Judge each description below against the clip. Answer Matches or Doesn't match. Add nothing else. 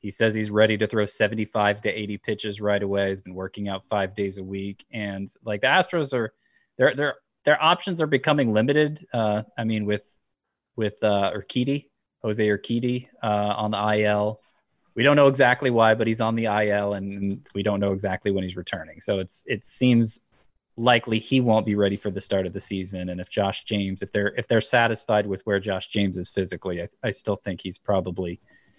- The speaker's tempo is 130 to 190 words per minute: Doesn't match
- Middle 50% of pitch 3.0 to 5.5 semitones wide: Doesn't match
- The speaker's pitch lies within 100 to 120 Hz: Matches